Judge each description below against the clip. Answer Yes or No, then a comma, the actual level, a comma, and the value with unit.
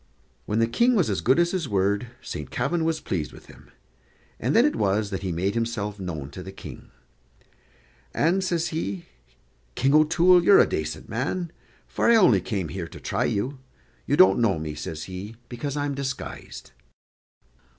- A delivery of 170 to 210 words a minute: Yes, average, 180 wpm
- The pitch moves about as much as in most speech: No, wide, 8.9 semitones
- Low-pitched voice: Yes, low, 115 Hz